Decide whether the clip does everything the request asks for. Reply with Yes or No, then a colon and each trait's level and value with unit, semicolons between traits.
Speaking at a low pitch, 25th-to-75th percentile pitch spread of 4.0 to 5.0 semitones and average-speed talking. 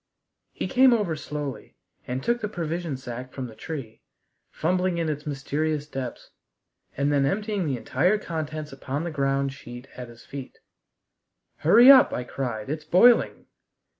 No: medium, 150 Hz; average, 4.6 semitones; average, 155 wpm